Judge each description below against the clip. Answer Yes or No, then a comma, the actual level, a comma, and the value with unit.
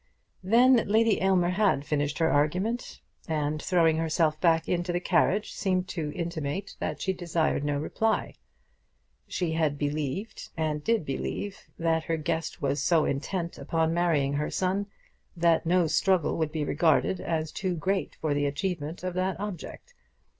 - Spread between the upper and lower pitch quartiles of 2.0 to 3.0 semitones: No, average, 3.5 semitones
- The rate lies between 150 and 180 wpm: Yes, average, 155 wpm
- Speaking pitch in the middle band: Yes, medium, 165 Hz